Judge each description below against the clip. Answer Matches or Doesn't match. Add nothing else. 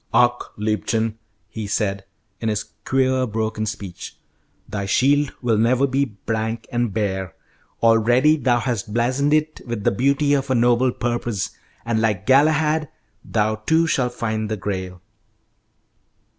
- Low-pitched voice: Matches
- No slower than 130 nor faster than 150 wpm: Matches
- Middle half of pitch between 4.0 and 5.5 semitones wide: Doesn't match